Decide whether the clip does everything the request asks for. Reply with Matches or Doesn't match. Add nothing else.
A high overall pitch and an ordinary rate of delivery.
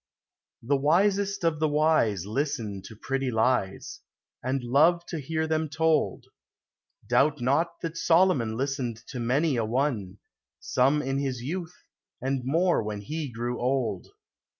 Doesn't match